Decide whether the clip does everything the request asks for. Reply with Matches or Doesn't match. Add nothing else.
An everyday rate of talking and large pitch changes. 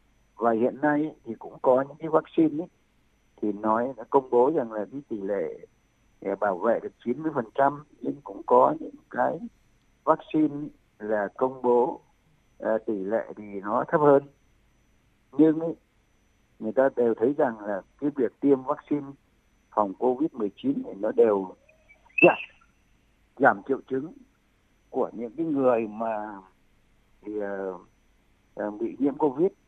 Doesn't match